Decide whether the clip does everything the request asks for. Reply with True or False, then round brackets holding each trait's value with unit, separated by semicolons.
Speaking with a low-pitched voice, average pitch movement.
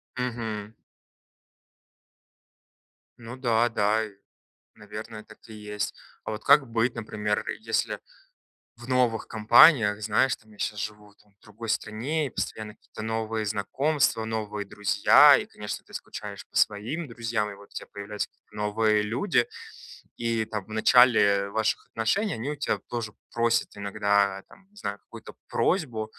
False (110 Hz; 2.2 semitones)